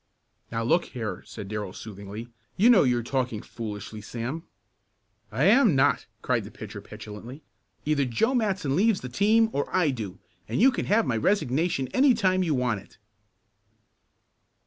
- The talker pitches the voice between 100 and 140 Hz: Yes, low, 135 Hz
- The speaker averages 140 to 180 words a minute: Yes, average, 160 wpm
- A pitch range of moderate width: No, wide, 8.9 semitones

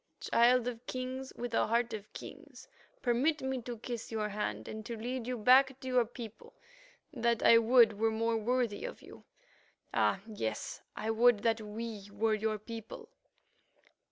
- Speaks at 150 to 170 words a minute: Yes, average, 165 wpm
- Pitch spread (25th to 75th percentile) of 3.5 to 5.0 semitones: No, narrow, 2.4 semitones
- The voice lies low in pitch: No, high, 230 Hz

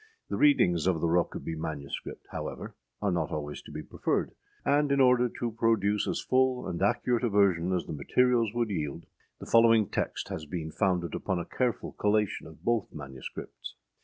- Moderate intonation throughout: No, wide, 6.1 semitones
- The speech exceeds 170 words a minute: Yes, average, 185 wpm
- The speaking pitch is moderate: No, low, 100 Hz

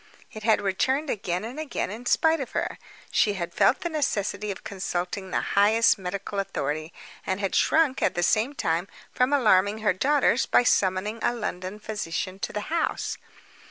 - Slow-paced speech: No, average, 175 wpm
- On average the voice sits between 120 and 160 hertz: No, high, 205 Hz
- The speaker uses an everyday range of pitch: Yes, average, 4.6 semitones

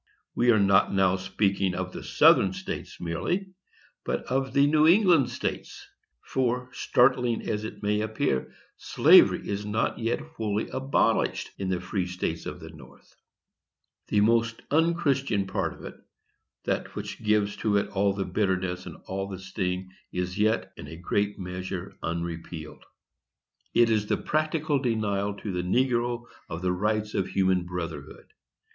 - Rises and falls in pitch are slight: No, average, 4.6 semitones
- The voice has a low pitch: Yes, low, 105 Hz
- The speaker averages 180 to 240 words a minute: No, average, 155 wpm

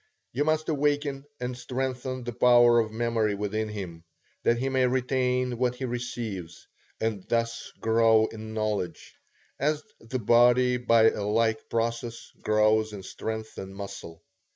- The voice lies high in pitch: No, low, 115 Hz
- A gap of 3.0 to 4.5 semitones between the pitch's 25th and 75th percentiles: No, narrow, 2.6 semitones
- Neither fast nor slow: Yes, average, 145 wpm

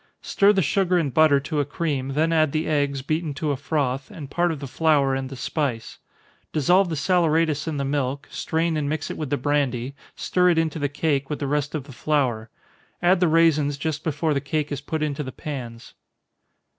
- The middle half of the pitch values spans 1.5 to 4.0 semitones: Yes, narrow, 2.5 semitones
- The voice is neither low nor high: Yes, medium, 150 Hz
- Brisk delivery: Yes, fast, 215 wpm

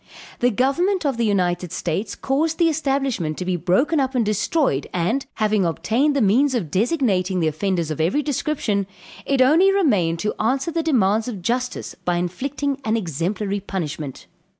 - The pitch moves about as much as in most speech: No, wide, 7.4 semitones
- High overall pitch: Yes, high, 220 Hz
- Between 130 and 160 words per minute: No, average, 170 wpm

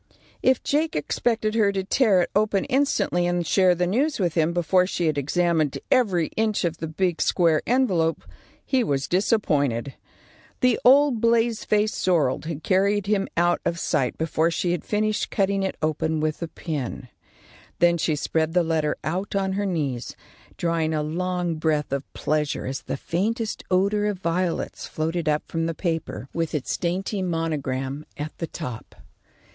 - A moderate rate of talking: Yes, average, 170 wpm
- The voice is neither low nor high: Yes, medium, 175 Hz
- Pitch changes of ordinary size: Yes, average, 4.3 semitones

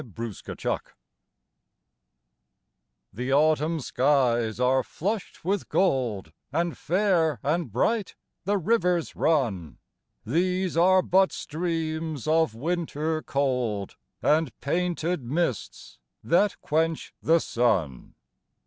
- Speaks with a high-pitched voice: No, medium, 155 Hz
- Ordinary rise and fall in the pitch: No, wide, 5.7 semitones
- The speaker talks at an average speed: No, slow, 95 wpm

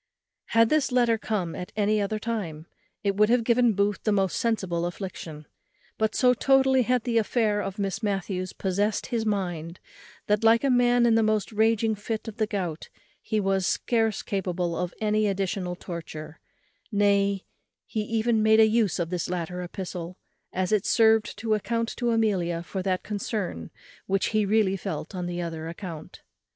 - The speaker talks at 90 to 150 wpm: No, average, 170 wpm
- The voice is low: No, high, 205 Hz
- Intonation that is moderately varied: Yes, average, 3.5 semitones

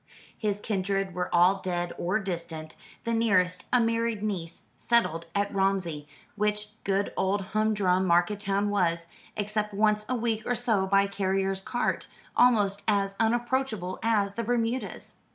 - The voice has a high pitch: Yes, high, 200 Hz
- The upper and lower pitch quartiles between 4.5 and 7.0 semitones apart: No, average, 2.8 semitones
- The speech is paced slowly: No, average, 145 wpm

